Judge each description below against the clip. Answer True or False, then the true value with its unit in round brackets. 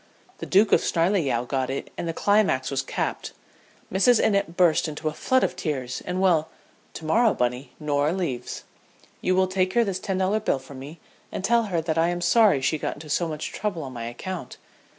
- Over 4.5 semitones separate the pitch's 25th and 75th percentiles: True (5.0 semitones)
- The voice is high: False (170 Hz)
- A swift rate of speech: True (210 wpm)